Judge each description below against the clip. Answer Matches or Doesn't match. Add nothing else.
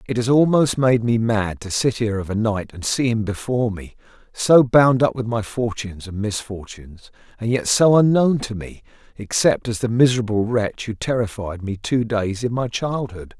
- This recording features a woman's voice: Doesn't match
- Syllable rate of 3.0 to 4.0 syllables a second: Doesn't match